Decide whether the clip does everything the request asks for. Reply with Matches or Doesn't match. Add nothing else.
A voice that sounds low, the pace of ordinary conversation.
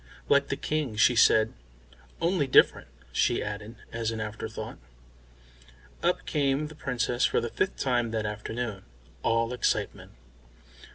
Doesn't match